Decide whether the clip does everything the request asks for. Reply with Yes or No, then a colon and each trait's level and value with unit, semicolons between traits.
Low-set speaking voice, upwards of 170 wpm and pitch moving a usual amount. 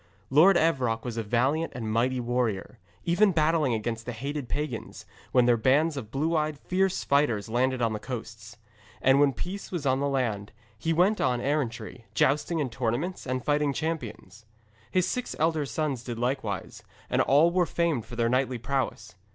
Yes: low, 130 Hz; average, 185 wpm; average, 4.8 semitones